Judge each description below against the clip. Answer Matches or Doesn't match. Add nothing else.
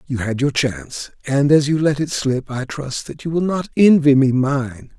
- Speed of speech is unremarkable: Doesn't match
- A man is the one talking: Matches